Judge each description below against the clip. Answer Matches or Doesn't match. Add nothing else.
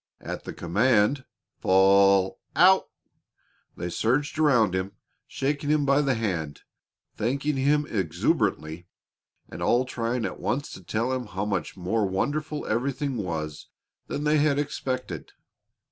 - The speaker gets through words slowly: Matches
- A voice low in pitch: Matches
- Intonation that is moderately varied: Doesn't match